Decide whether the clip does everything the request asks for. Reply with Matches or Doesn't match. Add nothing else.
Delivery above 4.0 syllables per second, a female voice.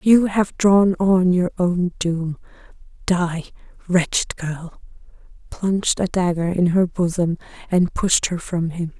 Doesn't match